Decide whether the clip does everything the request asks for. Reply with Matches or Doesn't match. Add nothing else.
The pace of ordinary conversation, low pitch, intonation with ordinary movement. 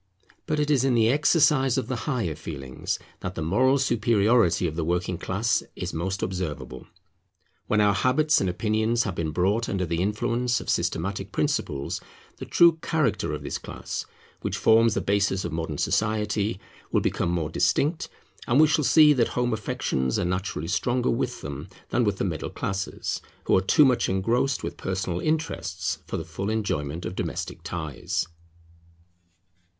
Doesn't match